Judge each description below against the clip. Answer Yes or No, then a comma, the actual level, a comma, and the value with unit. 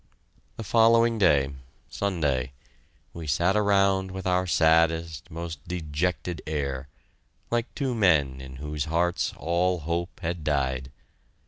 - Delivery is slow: Yes, slow, 120 wpm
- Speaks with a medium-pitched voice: No, very low, 85 Hz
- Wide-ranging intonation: No, average, 4.2 semitones